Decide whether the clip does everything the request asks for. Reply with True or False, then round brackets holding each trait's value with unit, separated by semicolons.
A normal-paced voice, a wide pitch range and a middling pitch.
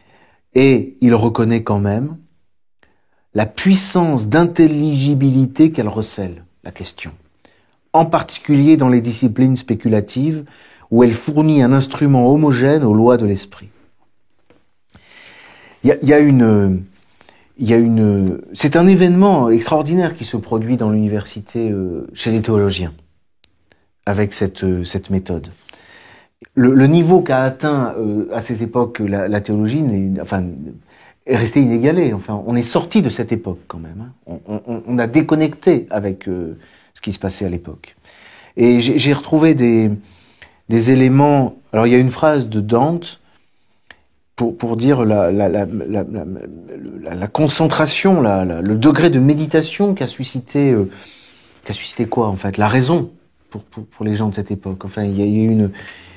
False (160 wpm; 5.9 semitones; 115 Hz)